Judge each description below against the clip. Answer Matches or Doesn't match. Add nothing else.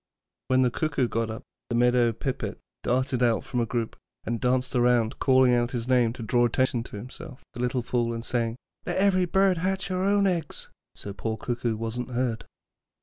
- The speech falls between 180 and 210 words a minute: Matches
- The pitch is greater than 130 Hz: Doesn't match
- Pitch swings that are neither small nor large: Doesn't match